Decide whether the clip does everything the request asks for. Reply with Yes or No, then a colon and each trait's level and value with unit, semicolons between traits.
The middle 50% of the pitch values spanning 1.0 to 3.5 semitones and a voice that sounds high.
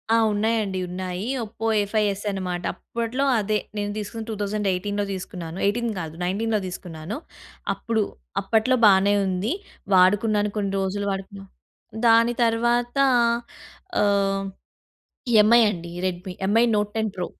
Yes: average, 2.9 semitones; high, 205 Hz